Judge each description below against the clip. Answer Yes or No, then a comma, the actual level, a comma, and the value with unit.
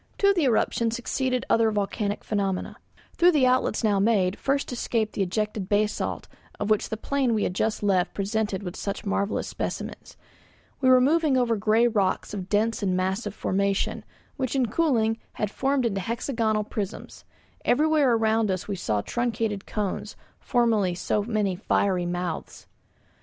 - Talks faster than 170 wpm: No, average, 155 wpm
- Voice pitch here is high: Yes, high, 215 Hz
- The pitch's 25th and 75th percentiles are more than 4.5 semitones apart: No, average, 3.5 semitones